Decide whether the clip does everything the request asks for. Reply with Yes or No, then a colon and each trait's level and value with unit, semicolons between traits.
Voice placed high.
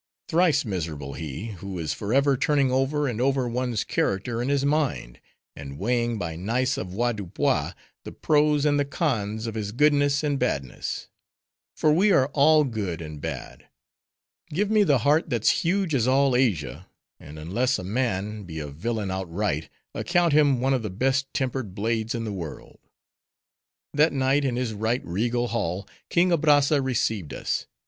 No: low, 120 Hz